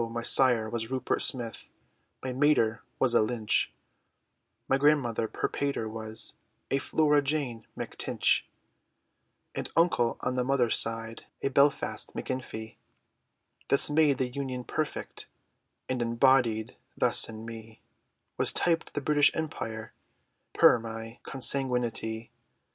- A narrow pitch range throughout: No, average, 3.5 semitones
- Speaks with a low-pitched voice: Yes, low, 125 Hz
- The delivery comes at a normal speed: No, slow, 125 wpm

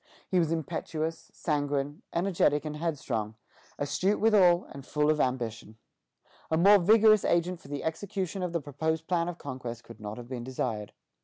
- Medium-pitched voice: Yes, medium, 160 Hz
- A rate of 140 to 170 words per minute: Yes, average, 165 wpm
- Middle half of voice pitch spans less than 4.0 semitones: No, average, 4.7 semitones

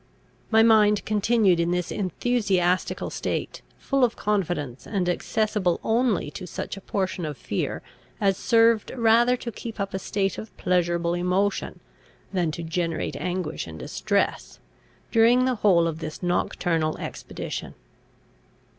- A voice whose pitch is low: No, high, 190 Hz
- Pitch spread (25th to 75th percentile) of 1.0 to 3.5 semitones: No, average, 4.3 semitones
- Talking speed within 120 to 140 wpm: Yes, slow, 135 wpm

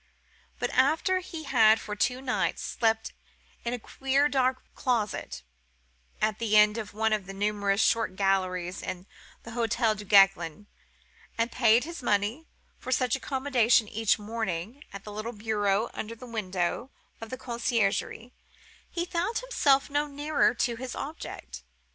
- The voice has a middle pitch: No, high, 225 Hz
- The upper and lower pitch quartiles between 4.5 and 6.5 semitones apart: No, average, 3.9 semitones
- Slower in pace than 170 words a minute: Yes, average, 150 wpm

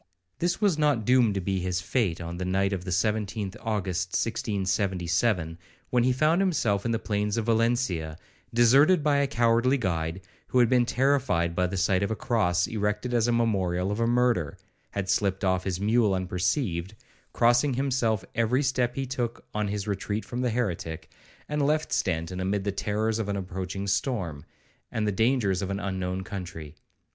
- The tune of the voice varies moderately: Yes, average, 4.6 semitones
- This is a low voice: Yes, low, 105 Hz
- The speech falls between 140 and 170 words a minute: No, average, 180 wpm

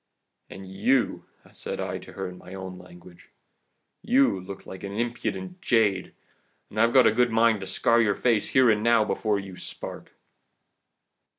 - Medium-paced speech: Yes, average, 165 wpm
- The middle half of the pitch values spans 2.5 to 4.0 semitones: Yes, average, 3.7 semitones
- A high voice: No, low, 105 Hz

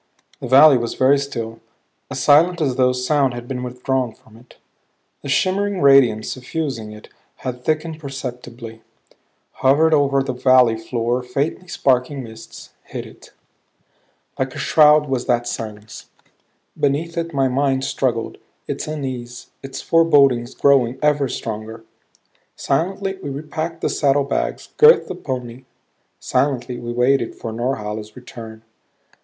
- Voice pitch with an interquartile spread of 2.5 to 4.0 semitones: Yes, average, 3.1 semitones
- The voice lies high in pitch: No, low, 130 Hz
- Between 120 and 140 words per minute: Yes, slow, 135 wpm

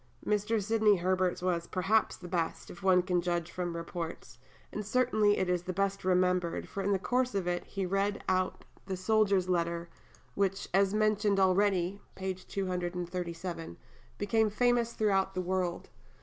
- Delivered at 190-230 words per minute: No, average, 165 wpm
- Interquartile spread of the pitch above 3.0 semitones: No, narrow, 2.4 semitones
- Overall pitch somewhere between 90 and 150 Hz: No, high, 190 Hz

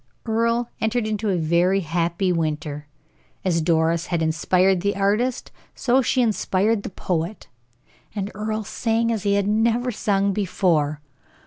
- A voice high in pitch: Yes, high, 195 Hz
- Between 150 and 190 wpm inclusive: No, average, 140 wpm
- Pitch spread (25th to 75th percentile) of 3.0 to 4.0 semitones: No, average, 4.5 semitones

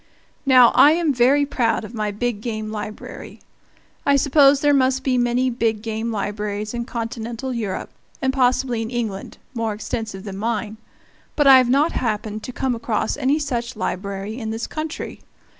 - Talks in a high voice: Yes, high, 235 Hz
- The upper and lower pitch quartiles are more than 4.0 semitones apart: No, average, 3.3 semitones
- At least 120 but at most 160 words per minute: No, average, 170 wpm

